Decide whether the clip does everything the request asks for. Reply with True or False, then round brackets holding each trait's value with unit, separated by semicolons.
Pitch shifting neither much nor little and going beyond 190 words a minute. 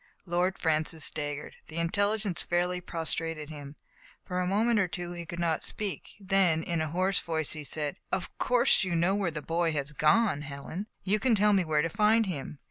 True (3.7 semitones; 200 wpm)